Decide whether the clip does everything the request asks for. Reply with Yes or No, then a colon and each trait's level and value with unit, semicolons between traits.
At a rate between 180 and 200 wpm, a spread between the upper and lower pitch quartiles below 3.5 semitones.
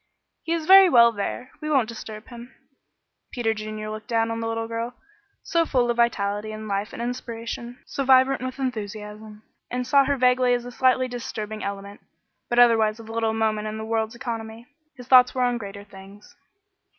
Yes: average, 185 wpm; narrow, 2.6 semitones